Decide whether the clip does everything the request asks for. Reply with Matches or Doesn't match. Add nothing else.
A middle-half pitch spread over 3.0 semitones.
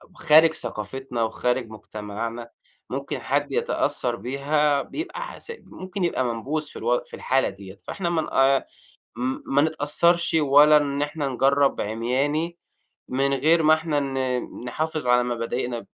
Matches